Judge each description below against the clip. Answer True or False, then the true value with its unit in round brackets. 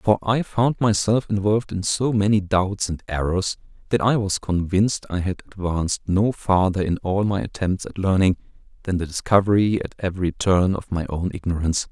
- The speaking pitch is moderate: False (95 Hz)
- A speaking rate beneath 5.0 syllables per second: False (5.2 syllables/s)